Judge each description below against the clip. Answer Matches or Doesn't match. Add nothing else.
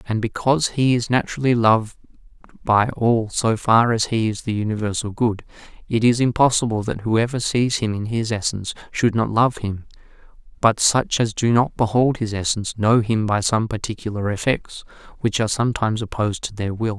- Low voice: Matches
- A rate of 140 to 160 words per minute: Doesn't match